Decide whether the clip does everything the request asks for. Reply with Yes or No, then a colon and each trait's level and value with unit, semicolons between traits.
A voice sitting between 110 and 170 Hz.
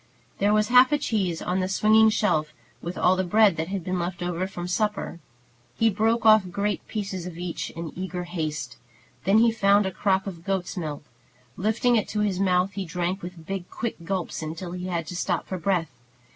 No: medium, 185 Hz